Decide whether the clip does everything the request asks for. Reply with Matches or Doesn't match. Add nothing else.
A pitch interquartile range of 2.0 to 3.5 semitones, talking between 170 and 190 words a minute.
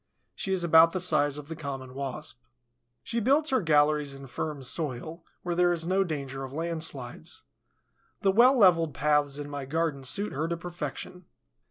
Doesn't match